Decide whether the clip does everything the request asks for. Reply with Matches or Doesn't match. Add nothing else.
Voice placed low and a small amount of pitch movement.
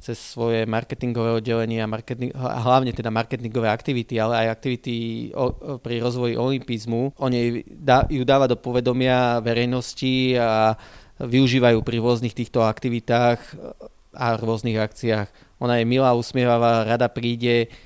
Matches